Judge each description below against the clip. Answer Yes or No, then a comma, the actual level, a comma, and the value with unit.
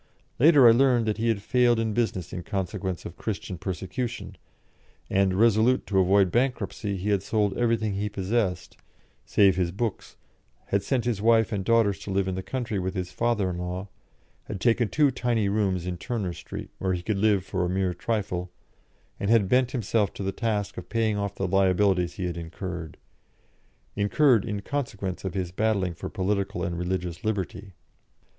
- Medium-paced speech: Yes, average, 180 wpm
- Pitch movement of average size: Yes, average, 3.4 semitones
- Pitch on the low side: Yes, low, 100 Hz